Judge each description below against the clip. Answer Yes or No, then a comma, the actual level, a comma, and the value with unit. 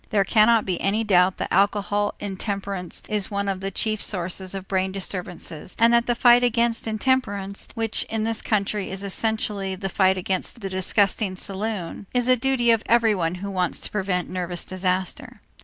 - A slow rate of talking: No, average, 175 wpm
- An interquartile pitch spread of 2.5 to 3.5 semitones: Yes, average, 2.9 semitones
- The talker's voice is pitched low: No, high, 200 Hz